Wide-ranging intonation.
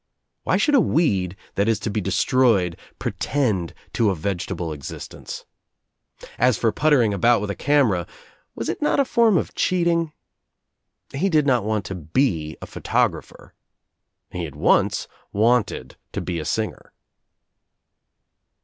Yes: wide, 7.4 semitones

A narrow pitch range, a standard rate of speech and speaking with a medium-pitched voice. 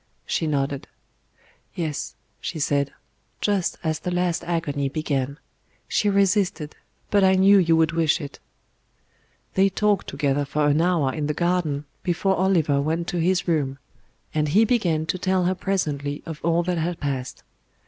No: average, 3.9 semitones; average, 160 wpm; medium, 165 Hz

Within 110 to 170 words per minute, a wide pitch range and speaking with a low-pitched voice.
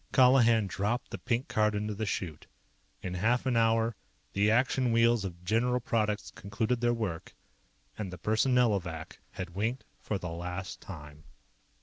No: average, 155 wpm; average, 3.9 semitones; low, 110 Hz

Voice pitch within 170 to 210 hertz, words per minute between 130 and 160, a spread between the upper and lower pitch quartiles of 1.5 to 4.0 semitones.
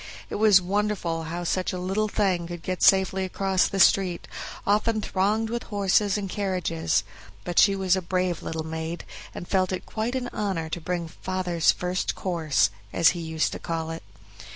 No: medium, 185 Hz; average, 180 wpm; average, 2.8 semitones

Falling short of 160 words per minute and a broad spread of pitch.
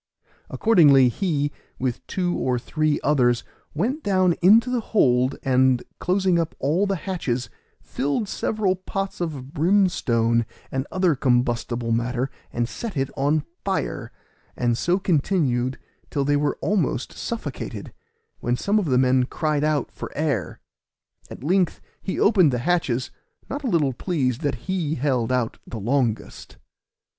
Yes: average, 145 wpm; wide, 6.5 semitones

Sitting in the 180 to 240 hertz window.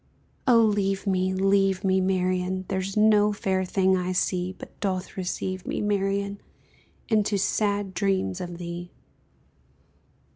Yes: high, 190 Hz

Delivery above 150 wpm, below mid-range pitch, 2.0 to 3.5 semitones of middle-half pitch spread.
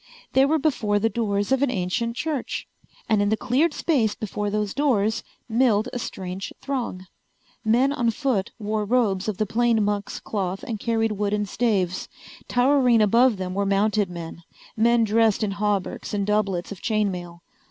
No: average, 170 wpm; high, 215 Hz; average, 3.1 semitones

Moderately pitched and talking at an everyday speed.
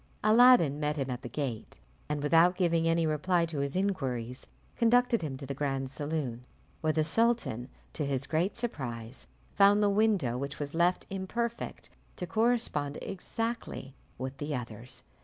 Yes: medium, 155 Hz; average, 160 wpm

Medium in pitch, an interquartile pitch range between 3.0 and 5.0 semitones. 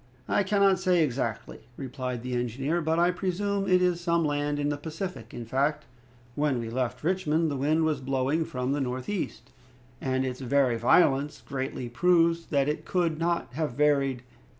Yes: medium, 145 Hz; average, 4.6 semitones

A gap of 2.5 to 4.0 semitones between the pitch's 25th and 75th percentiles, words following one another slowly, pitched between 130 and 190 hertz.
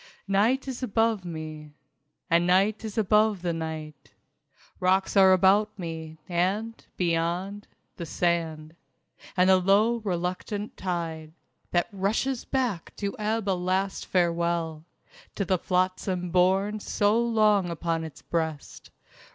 Yes: average, 3.6 semitones; slow, 125 wpm; medium, 185 Hz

